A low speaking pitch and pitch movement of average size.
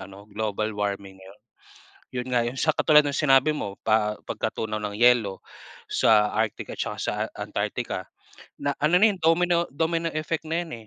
No: low, 120 Hz; wide, 6.9 semitones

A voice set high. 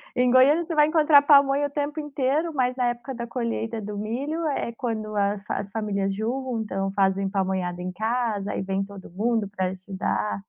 Yes: high, 225 Hz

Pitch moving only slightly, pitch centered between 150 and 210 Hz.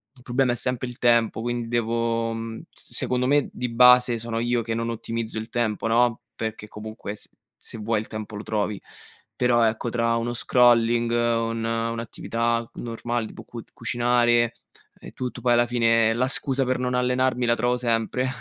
No: narrow, 1.2 semitones; low, 115 Hz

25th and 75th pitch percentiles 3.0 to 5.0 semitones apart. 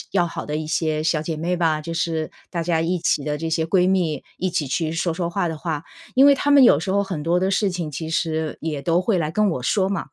No: narrow, 2.6 semitones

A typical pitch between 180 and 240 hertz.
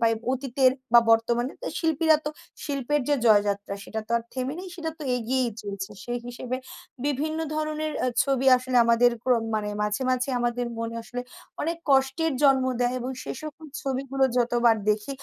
No: very high, 255 Hz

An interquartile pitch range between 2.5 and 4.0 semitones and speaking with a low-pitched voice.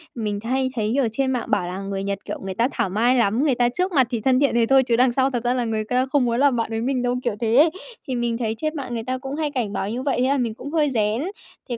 No: average, 2.9 semitones; high, 245 Hz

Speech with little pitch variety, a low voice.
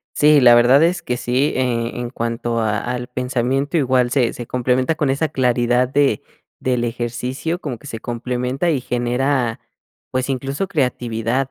Yes: narrow, 2.2 semitones; low, 125 Hz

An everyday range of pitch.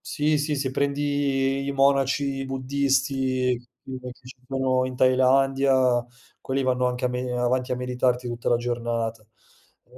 No: narrow, 1.5 semitones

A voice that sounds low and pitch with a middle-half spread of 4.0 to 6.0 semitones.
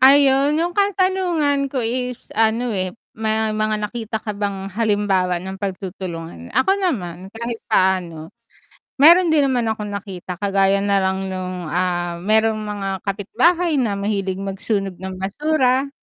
No: high, 210 Hz; average, 4.9 semitones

